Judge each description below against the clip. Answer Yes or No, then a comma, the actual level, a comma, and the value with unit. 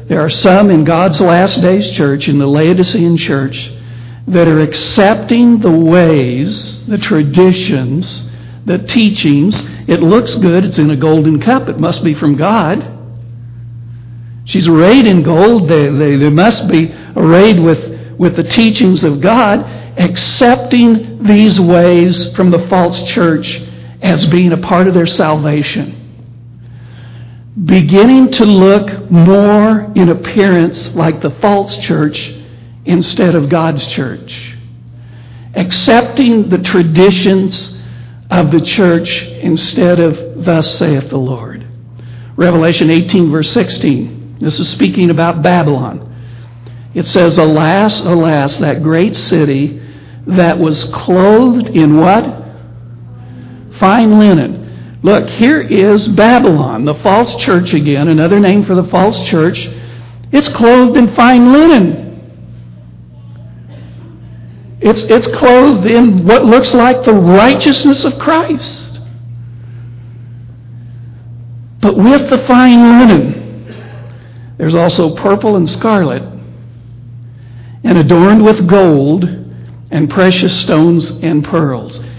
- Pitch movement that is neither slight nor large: No, wide, 8.4 semitones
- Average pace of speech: No, slow, 120 wpm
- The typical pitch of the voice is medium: Yes, medium, 165 Hz